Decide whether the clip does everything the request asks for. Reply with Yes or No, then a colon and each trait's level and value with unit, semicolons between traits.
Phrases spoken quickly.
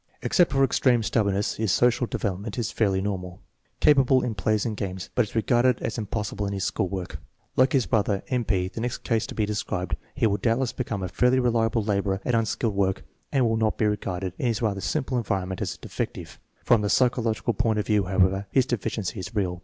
Yes: fast, 225 wpm